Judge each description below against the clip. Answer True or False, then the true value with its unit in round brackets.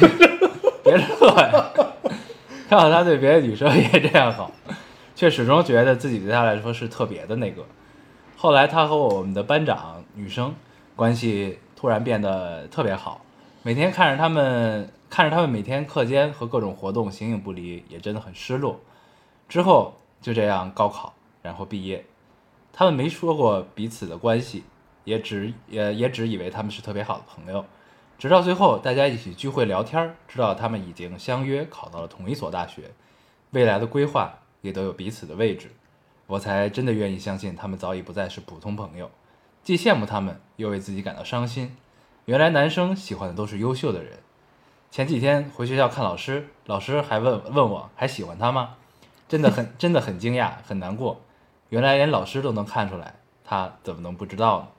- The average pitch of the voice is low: True (115 Hz)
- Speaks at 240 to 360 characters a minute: True (280 characters per minute)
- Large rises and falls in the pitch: True (6.0 semitones)